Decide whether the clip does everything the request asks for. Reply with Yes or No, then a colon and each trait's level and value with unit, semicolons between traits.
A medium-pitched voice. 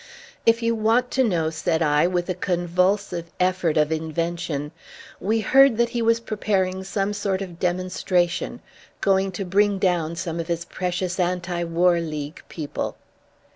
Yes: medium, 180 Hz